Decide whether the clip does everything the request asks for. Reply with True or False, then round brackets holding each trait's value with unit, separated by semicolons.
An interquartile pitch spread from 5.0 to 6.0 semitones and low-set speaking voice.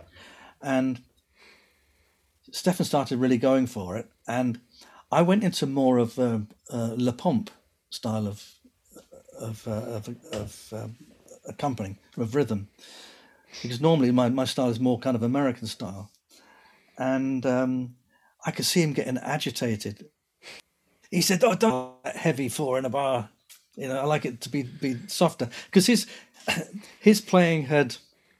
False (4.4 semitones; 130 Hz)